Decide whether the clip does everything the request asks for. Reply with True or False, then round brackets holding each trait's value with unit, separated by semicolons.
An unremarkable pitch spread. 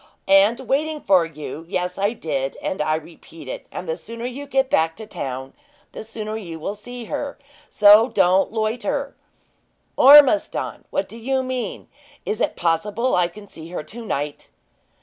False (6.9 semitones)